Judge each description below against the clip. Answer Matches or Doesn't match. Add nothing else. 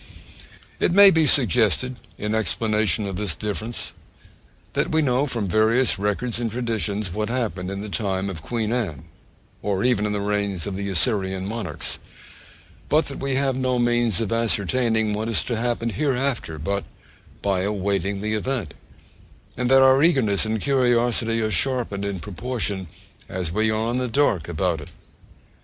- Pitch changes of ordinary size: Matches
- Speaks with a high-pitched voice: Doesn't match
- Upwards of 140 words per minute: Matches